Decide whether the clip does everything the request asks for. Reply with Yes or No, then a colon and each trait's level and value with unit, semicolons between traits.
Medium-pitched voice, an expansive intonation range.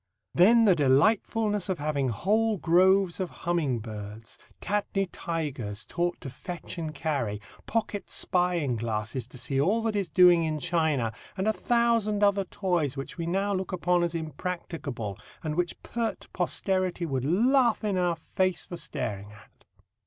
Yes: medium, 175 Hz; wide, 5.9 semitones